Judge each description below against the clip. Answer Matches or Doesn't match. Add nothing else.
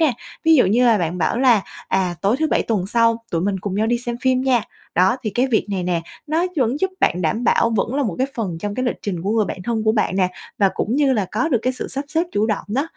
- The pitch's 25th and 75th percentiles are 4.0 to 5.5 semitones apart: Matches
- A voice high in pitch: Matches